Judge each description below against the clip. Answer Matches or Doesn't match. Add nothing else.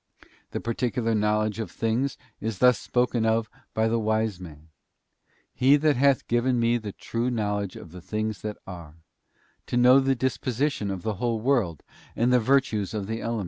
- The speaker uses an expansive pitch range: Doesn't match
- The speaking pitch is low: Matches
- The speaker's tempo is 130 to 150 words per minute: Doesn't match